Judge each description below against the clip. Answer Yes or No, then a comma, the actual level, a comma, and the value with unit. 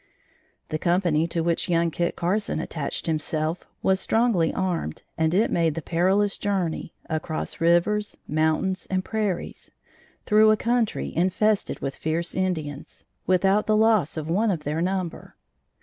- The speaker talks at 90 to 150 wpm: Yes, average, 145 wpm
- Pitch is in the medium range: Yes, medium, 175 Hz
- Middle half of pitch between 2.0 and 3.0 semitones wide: No, average, 3.8 semitones